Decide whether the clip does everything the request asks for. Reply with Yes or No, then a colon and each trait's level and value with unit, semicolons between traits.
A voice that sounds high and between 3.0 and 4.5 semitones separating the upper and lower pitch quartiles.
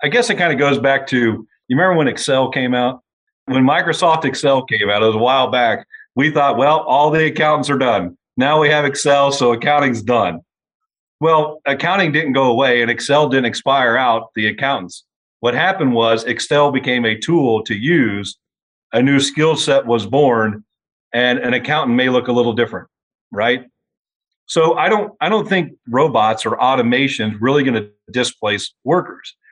No: low, 135 Hz; average, 4.1 semitones